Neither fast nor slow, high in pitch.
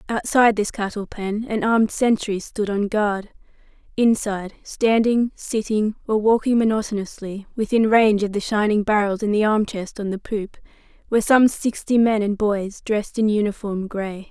Yes: average, 165 wpm; high, 215 Hz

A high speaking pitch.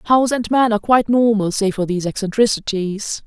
Yes: high, 215 Hz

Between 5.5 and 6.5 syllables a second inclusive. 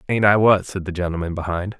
Yes: 6.2 syllables/s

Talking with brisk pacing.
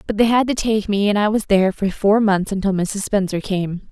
Yes: fast, 245 wpm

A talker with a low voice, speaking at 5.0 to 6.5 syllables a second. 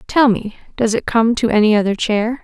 No: high, 225 Hz; 5.3 syllables/s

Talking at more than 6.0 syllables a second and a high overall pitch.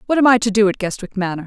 Yes: 7.6 syllables/s; high, 210 Hz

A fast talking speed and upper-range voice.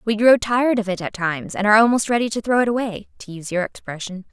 Yes: fast, 265 wpm; high, 215 Hz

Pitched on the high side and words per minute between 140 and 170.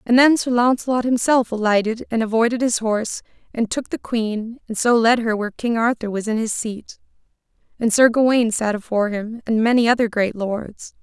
No: high, 230 Hz; average, 195 wpm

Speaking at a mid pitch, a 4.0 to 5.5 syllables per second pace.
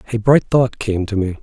No: low, 110 Hz; 5.1 syllables/s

